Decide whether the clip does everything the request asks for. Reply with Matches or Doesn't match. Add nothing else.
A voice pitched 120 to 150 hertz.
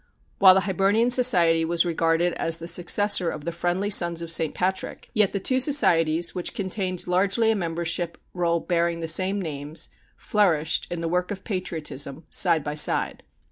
Doesn't match